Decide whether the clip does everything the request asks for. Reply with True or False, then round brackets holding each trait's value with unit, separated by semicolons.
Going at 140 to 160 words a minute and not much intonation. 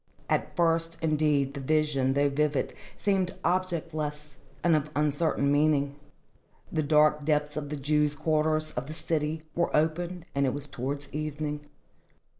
True (145 wpm; 1.5 semitones)